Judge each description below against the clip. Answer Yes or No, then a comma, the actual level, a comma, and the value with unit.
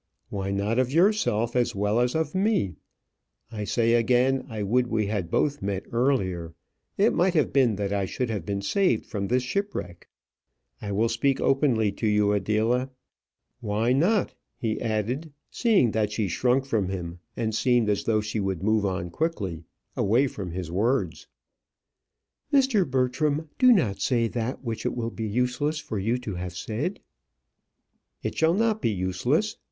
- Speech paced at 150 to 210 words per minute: Yes, average, 170 wpm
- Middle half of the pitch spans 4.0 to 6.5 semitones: Yes, average, 4.8 semitones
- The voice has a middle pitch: No, low, 115 Hz